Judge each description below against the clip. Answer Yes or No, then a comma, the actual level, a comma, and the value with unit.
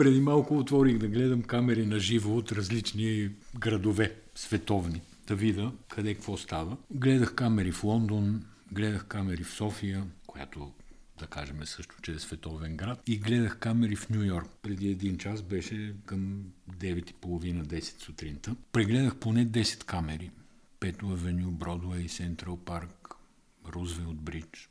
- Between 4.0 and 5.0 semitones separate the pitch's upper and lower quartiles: Yes, average, 4.4 semitones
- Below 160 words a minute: Yes, average, 140 wpm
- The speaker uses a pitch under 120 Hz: Yes, low, 100 Hz